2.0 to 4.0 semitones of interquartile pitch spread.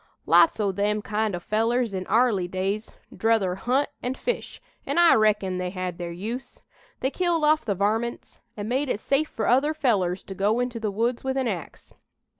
No: average, 4.6 semitones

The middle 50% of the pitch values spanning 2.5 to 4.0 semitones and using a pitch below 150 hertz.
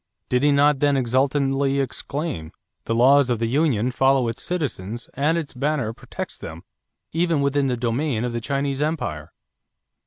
Yes: average, 3.1 semitones; low, 135 Hz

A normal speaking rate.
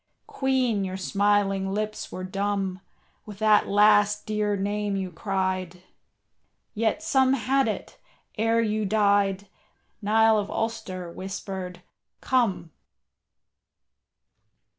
No: slow, 100 wpm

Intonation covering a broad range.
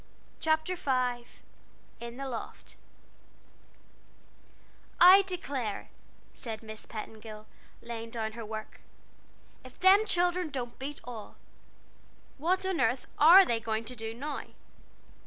Yes: wide, 6.6 semitones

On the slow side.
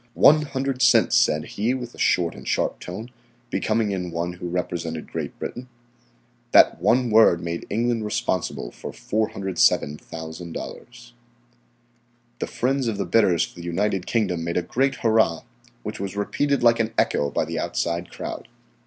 No: average, 155 wpm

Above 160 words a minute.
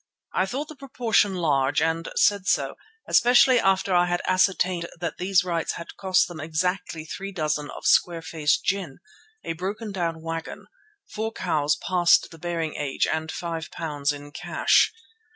No: average, 155 wpm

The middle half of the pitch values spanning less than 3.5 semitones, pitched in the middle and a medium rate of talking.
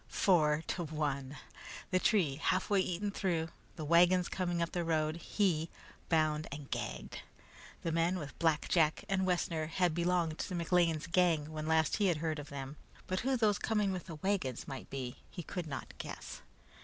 Yes: average, 3.0 semitones; medium, 165 Hz; average, 180 wpm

